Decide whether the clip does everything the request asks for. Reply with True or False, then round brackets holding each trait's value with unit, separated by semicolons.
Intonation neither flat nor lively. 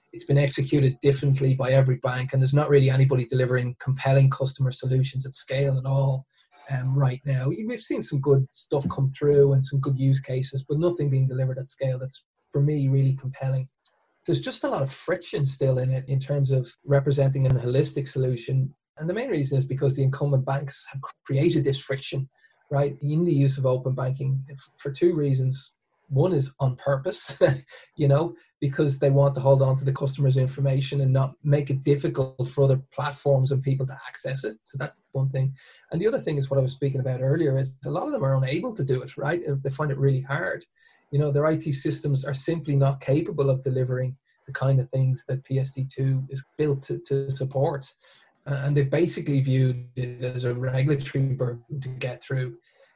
False (1.2 semitones)